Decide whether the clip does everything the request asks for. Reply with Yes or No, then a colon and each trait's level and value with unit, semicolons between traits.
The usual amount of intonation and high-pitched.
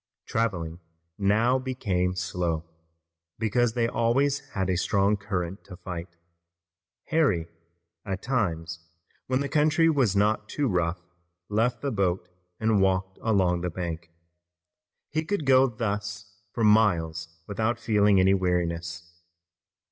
No: average, 4.6 semitones; low, 100 Hz